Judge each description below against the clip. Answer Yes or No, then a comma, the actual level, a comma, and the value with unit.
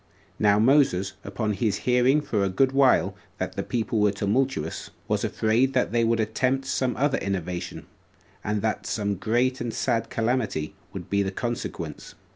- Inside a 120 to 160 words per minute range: No, average, 170 wpm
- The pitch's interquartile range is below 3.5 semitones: No, average, 3.9 semitones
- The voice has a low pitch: Yes, low, 115 Hz